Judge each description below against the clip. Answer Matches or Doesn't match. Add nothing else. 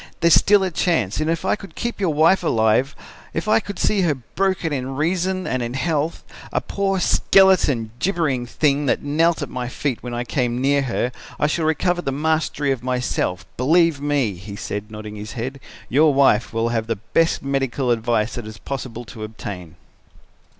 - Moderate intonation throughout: Doesn't match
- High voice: Doesn't match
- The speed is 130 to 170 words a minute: Doesn't match